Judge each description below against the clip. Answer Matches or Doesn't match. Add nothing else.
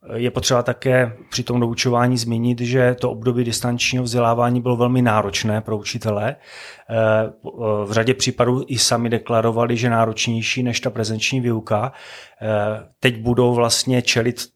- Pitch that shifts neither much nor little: Doesn't match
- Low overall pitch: Matches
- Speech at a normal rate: Matches